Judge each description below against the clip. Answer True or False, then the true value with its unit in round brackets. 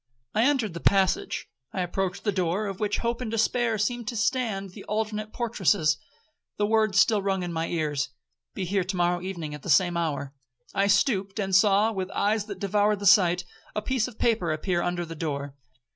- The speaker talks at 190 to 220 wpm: True (200 wpm)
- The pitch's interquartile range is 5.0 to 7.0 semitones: False (3.5 semitones)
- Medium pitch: False (195 Hz)